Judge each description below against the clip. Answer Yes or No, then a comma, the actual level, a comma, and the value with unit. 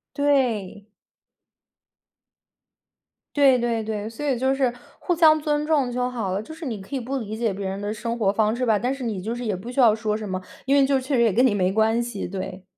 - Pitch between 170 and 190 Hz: No, high, 235 Hz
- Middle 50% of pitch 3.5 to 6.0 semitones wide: Yes, average, 4.1 semitones